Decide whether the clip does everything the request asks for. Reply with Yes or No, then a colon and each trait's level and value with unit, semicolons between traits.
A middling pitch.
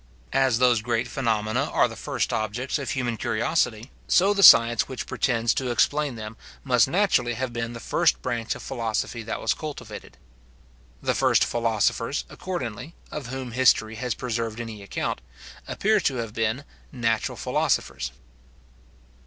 No: low, 120 Hz